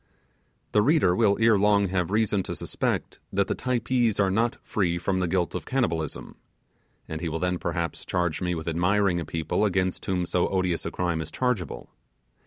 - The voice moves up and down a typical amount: Yes, average, 3.2 semitones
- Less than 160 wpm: No, average, 190 wpm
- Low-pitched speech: Yes, very low, 95 Hz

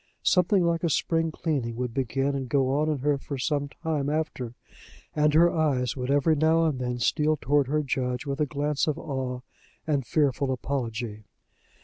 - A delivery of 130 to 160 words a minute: No, average, 185 wpm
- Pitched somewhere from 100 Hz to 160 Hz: Yes, medium, 140 Hz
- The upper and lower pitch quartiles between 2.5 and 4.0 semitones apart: Yes, average, 3.3 semitones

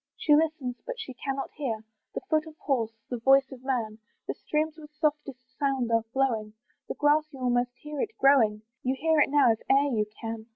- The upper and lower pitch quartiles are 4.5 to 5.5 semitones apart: No, average, 3.9 semitones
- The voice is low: No, very high, 270 Hz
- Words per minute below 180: No, fast, 205 wpm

